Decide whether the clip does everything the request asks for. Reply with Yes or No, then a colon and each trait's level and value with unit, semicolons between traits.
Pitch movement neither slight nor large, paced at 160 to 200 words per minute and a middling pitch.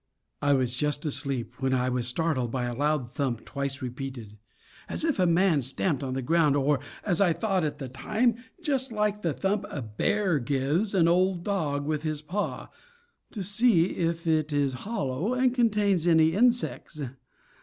No: wide, 6.5 semitones; average, 175 wpm; medium, 155 Hz